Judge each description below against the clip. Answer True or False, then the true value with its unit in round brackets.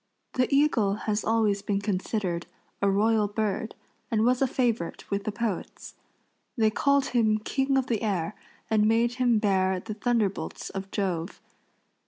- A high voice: True (215 Hz)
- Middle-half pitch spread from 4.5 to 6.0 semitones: False (2.9 semitones)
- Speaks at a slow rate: False (155 wpm)